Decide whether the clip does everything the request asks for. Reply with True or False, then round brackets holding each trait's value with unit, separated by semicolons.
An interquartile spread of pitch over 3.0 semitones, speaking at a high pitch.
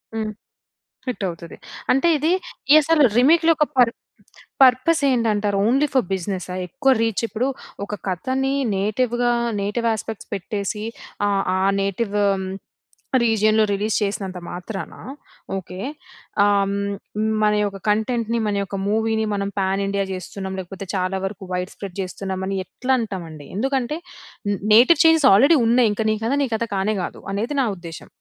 True (4.1 semitones; 210 Hz)